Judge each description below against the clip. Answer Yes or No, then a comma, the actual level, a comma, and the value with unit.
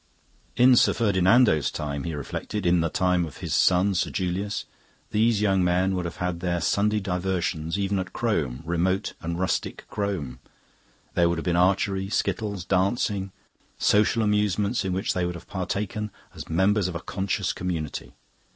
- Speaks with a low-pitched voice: Yes, very low, 95 Hz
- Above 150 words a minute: Yes, average, 165 wpm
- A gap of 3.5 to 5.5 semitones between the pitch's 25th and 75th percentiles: No, average, 2.8 semitones